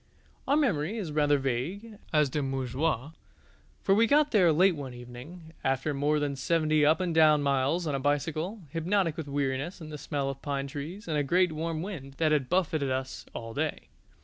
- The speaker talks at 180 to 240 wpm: Yes, average, 195 wpm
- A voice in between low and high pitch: Yes, medium, 150 Hz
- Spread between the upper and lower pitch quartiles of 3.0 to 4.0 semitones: Yes, average, 3.7 semitones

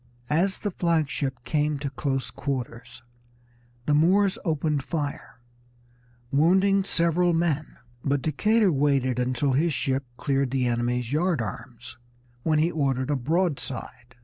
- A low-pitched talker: No, medium, 145 Hz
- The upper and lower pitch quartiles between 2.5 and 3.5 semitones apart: No, average, 4.2 semitones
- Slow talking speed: Yes, slow, 130 wpm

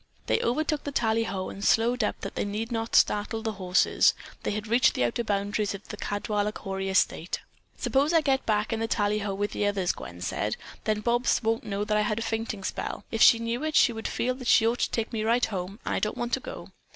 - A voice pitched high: Yes, high, 220 Hz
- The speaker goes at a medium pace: No, fast, 240 wpm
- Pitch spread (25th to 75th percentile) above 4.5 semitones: No, narrow, 2.4 semitones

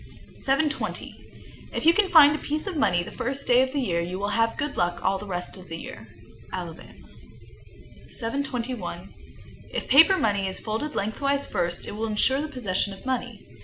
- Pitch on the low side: No, high, 225 Hz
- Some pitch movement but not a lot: No, wide, 6.9 semitones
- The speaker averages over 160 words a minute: Yes, average, 185 wpm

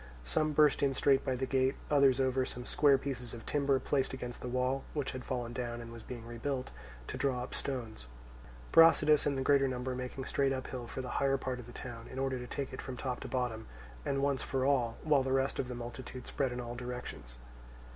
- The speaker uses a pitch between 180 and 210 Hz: No, low, 130 Hz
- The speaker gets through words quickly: Yes, fast, 225 wpm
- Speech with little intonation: Yes, narrow, 1.8 semitones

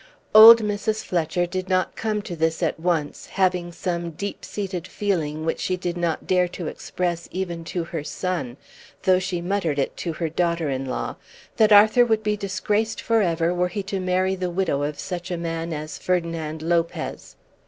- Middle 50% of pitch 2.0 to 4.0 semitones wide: Yes, narrow, 2.6 semitones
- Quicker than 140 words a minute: Yes, average, 185 wpm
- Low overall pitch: No, medium, 180 Hz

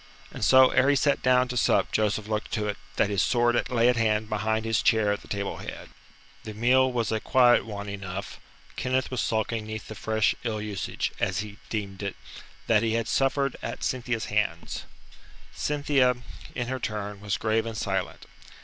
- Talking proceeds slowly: No, average, 190 wpm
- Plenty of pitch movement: No, average, 2.9 semitones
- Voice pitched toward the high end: No, low, 110 Hz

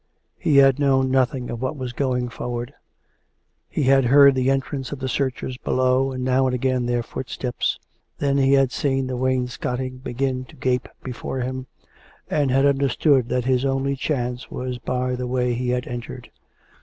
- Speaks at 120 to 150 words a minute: No, average, 180 wpm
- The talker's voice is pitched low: Yes, low, 130 Hz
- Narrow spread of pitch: Yes, narrow, 1.3 semitones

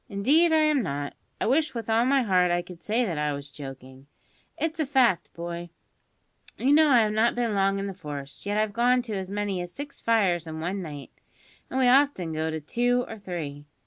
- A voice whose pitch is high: Yes, high, 200 Hz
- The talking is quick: Yes, fast, 220 wpm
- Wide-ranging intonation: Yes, wide, 6.7 semitones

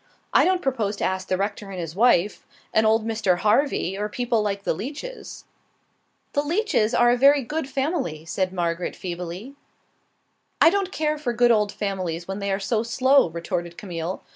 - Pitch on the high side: Yes, high, 210 Hz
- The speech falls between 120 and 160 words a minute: No, average, 185 wpm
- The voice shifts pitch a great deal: Yes, wide, 6.1 semitones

